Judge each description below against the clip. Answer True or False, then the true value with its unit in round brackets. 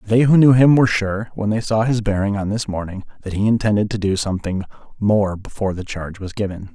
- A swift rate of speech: True (230 wpm)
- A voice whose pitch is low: True (105 Hz)